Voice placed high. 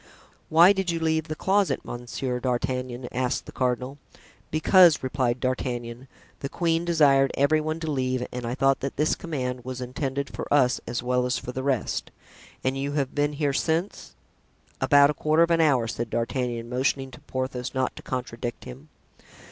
No: low, 135 Hz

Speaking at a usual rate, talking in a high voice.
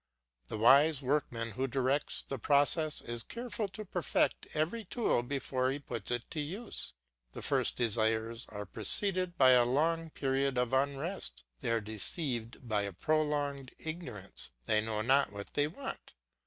No: average, 155 wpm; low, 135 Hz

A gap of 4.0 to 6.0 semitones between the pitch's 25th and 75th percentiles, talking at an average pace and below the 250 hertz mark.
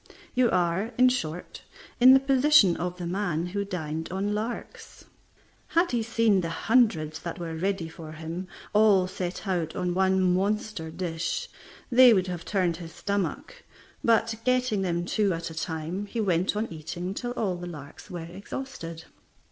Yes: average, 4.5 semitones; average, 165 wpm; medium, 185 Hz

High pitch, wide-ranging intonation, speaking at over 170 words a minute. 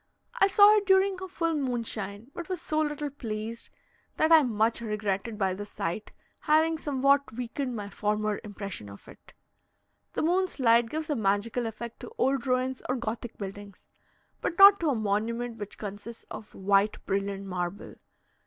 No: high, 235 Hz; wide, 6.4 semitones; average, 165 wpm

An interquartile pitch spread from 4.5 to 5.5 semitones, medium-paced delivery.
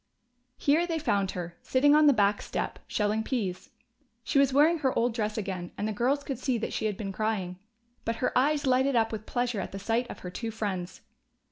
No: average, 4.8 semitones; fast, 220 wpm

